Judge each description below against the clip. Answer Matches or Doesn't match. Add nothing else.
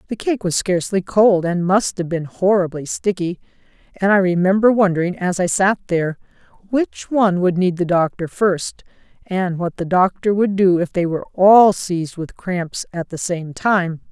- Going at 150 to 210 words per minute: Matches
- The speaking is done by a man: Doesn't match